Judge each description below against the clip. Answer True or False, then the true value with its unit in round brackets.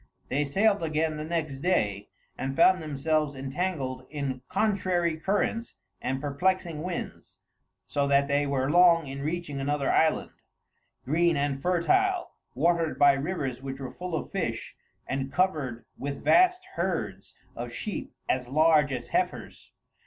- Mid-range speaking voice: True (150 Hz)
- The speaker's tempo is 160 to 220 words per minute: False (140 wpm)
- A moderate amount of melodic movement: True (4.3 semitones)